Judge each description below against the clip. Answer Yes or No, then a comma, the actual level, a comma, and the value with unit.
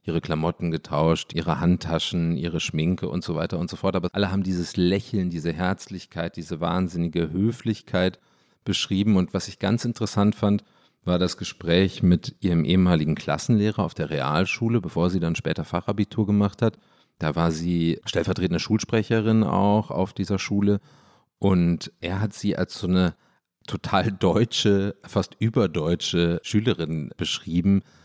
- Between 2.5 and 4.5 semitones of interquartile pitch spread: Yes, average, 3.2 semitones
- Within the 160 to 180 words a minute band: No, average, 150 wpm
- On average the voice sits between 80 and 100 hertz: Yes, very low, 95 Hz